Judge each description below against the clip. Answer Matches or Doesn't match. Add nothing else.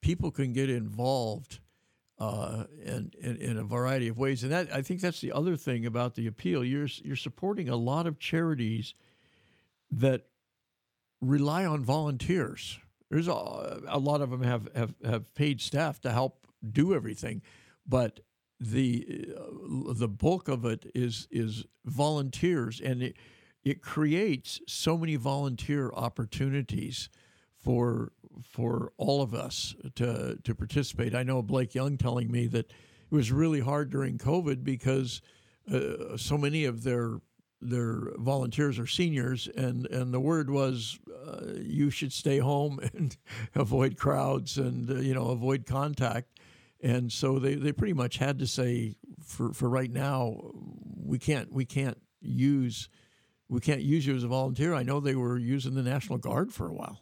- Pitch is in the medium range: Doesn't match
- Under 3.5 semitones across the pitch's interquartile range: Matches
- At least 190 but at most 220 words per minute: Doesn't match